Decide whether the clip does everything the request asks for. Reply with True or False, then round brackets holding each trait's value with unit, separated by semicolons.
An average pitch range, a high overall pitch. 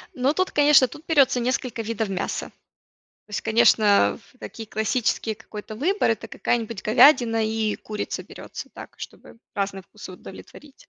True (3.4 semitones; 225 Hz)